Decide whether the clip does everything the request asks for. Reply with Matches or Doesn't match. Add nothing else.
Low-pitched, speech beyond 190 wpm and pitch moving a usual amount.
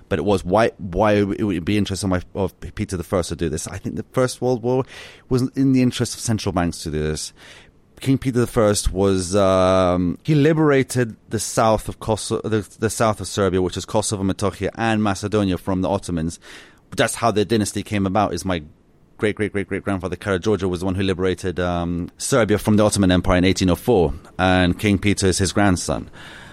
Matches